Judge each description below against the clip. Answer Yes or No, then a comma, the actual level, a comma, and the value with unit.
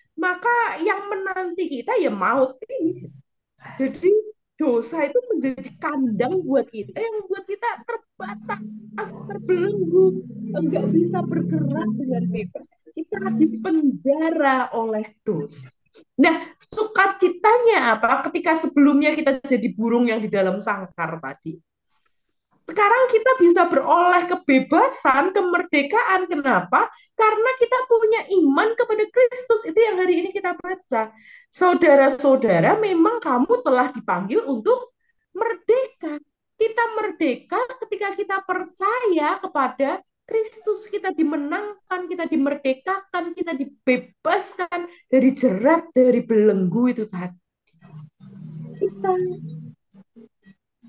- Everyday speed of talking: Yes, average, 105 wpm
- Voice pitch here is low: No, very high, 315 Hz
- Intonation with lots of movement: Yes, wide, 8.9 semitones